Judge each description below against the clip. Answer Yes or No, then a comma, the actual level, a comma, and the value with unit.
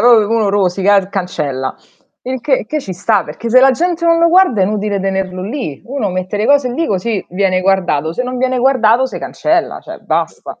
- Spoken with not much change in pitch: No, wide, 5.6 semitones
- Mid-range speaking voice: No, high, 215 Hz